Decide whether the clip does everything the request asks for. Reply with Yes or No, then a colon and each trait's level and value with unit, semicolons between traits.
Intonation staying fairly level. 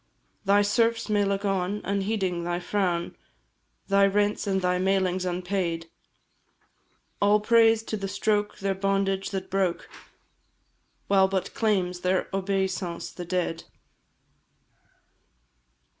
Yes: narrow, 2.0 semitones